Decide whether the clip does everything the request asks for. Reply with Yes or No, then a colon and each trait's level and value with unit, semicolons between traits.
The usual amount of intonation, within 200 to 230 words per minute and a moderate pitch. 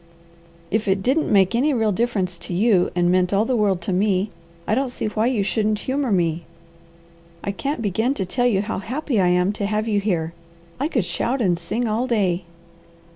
No: average, 4.4 semitones; fast, 205 wpm; high, 210 Hz